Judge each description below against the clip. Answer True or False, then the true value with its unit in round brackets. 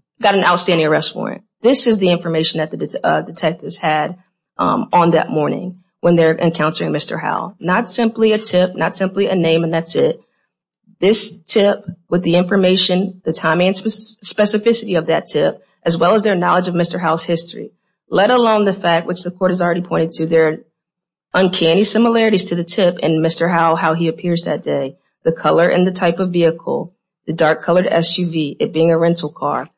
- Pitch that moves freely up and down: False (3.0 semitones)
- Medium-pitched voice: True (175 Hz)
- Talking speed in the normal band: True (195 wpm)